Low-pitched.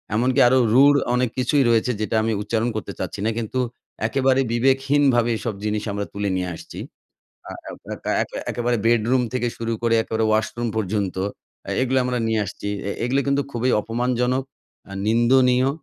Yes: low, 120 Hz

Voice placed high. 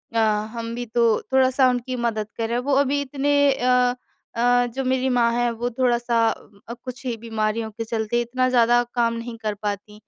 Yes: high, 240 Hz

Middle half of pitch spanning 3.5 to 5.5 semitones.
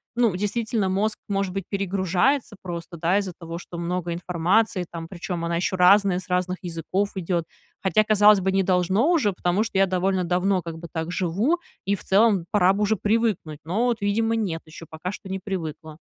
No: average, 2.9 semitones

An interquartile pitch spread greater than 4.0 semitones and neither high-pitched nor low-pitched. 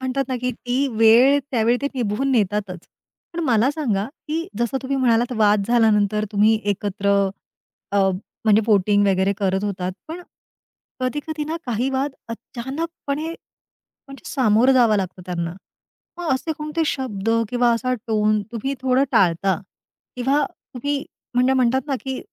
No: average, 4.4 semitones; high, 240 Hz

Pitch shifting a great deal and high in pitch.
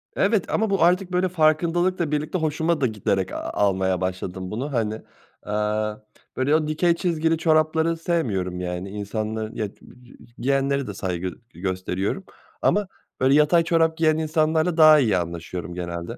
No: wide, 8.8 semitones; medium, 140 Hz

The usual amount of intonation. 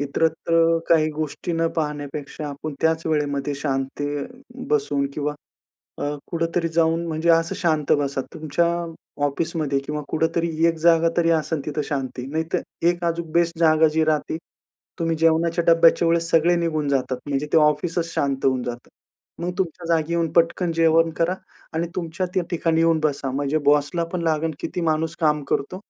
No: narrow, 2.1 semitones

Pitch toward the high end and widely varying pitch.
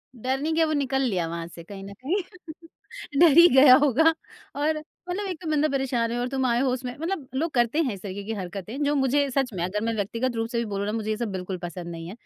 Yes: high, 245 Hz; wide, 6.1 semitones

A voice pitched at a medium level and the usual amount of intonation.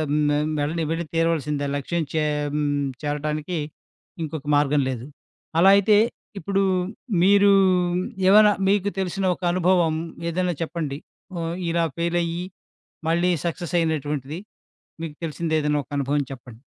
Yes: medium, 165 Hz; average, 3.0 semitones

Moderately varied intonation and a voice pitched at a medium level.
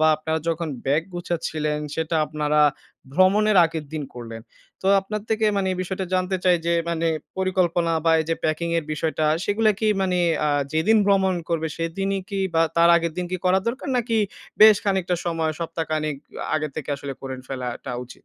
Yes: average, 3.4 semitones; medium, 170 Hz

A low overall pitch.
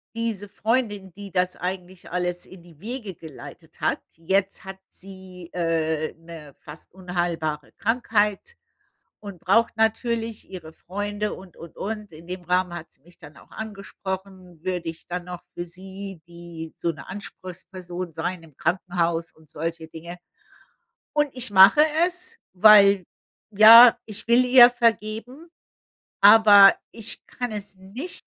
No: high, 190 Hz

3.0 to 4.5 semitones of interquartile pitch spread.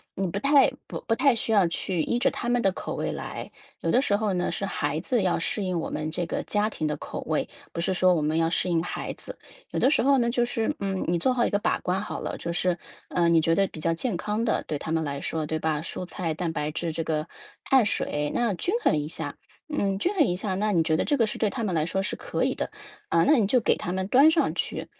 No: wide, 5.6 semitones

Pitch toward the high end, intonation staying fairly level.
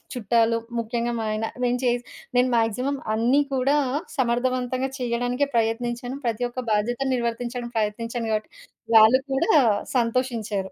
Yes: high, 240 Hz; narrow, 1.9 semitones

